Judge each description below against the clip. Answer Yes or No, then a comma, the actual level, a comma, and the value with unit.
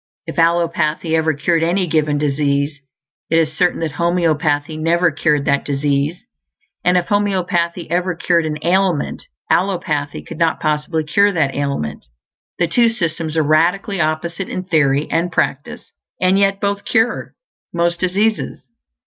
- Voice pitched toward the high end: No, medium, 165 Hz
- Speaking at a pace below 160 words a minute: Yes, average, 145 wpm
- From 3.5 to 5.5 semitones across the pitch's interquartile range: No, average, 3.0 semitones